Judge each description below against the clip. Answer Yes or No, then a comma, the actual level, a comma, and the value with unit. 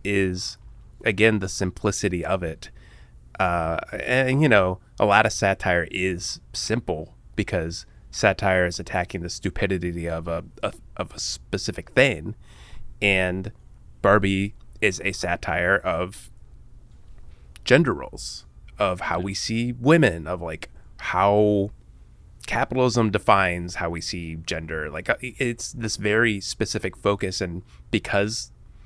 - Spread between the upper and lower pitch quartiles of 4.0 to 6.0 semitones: No, average, 3.4 semitones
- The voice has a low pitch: Yes, very low, 95 Hz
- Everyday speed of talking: No, slow, 125 wpm